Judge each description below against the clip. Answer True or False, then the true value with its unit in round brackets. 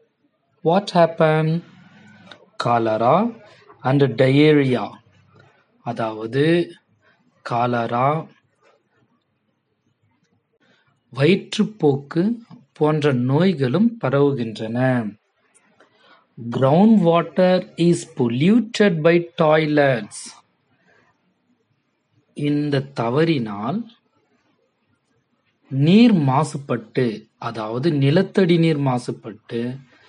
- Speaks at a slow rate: True (40 wpm)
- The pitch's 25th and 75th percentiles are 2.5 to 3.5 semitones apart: False (5.4 semitones)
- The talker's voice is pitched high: False (150 Hz)